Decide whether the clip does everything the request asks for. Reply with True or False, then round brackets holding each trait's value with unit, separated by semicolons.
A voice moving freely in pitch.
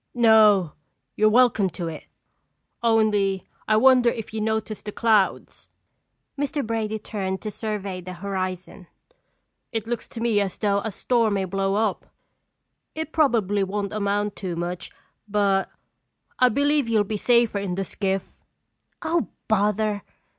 False (2.6 semitones)